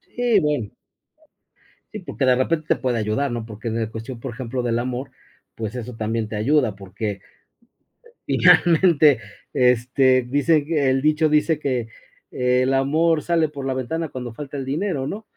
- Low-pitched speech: Yes, low, 130 Hz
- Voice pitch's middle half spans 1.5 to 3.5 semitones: No, average, 4.2 semitones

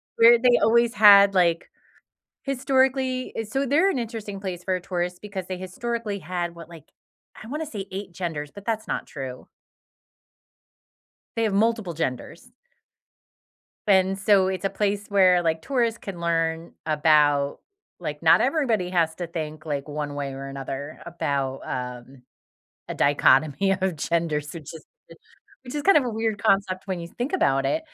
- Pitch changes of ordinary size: No, wide, 6.1 semitones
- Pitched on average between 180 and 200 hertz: Yes, medium, 185 Hz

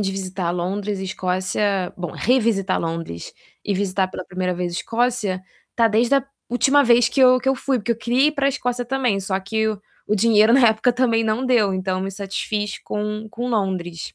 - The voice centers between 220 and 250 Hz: No, high, 210 Hz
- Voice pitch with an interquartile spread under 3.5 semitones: No, average, 4.2 semitones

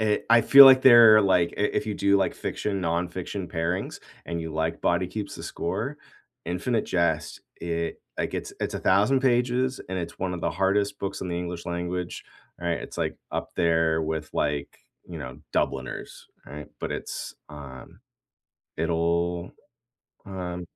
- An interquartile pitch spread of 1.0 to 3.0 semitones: No, average, 3.4 semitones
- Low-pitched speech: Yes, very low, 90 Hz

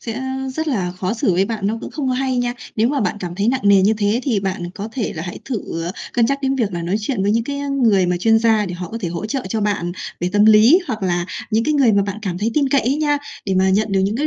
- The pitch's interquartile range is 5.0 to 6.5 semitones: No, average, 4.6 semitones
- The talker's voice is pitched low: No, high, 215 Hz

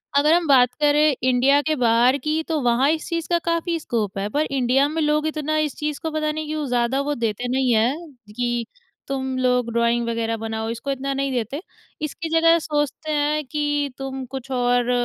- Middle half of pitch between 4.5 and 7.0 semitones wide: No, average, 3.8 semitones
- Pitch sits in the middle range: No, very high, 275 Hz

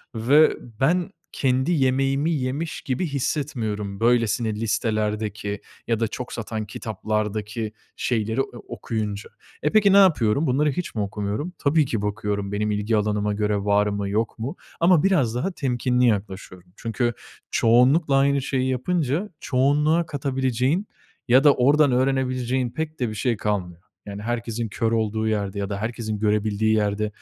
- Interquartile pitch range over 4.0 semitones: Yes, average, 4.4 semitones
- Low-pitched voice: Yes, low, 115 Hz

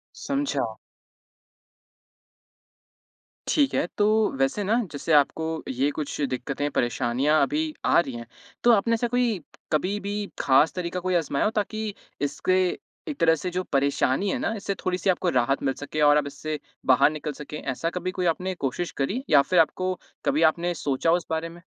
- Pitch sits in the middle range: Yes, medium, 160 Hz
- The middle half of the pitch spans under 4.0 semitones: No, average, 4.7 semitones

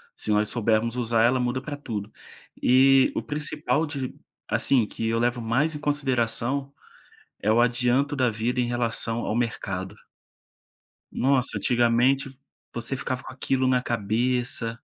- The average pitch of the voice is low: Yes, low, 125 Hz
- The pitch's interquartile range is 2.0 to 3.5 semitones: Yes, narrow, 2.6 semitones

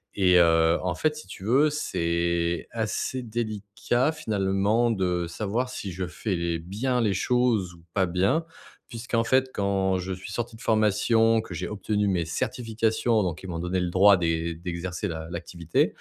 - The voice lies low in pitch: Yes, low, 100 Hz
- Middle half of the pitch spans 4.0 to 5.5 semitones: Yes, average, 4.6 semitones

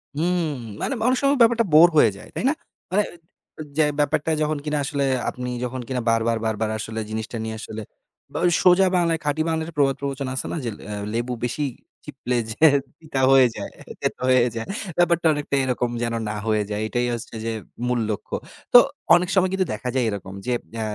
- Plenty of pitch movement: Yes, wide, 6.0 semitones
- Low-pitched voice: Yes, low, 130 Hz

